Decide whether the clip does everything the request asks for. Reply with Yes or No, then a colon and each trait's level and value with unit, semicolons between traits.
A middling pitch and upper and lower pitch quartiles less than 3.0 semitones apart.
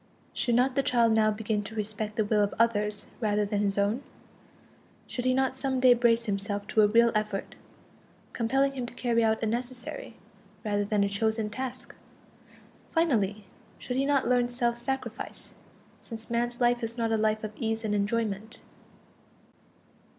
No: high, 225 Hz; narrow, 2.6 semitones